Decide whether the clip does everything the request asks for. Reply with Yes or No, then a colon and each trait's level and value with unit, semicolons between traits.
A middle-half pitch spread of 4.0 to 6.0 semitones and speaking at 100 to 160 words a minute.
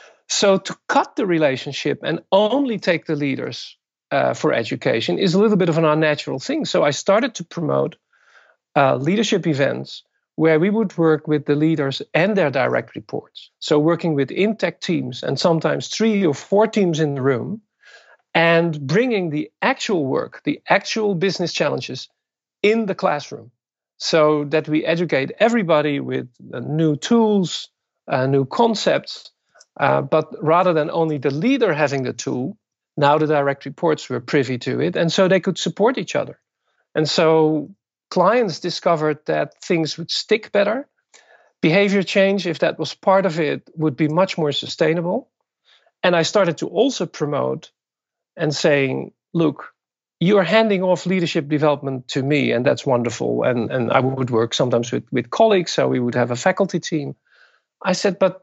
No: average, 4.9 semitones; average, 170 wpm